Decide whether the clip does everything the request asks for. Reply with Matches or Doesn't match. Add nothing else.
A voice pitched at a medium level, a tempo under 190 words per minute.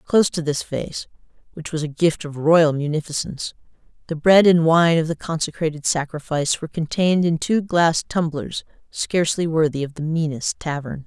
Matches